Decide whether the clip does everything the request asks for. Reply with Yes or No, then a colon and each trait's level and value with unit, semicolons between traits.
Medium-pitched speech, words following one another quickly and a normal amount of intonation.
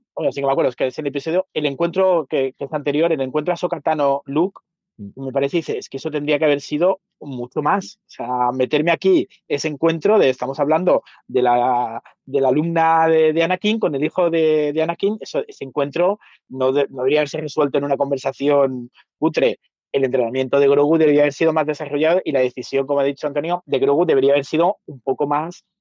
Yes: medium, 150 Hz; fast, 220 wpm; average, 3.1 semitones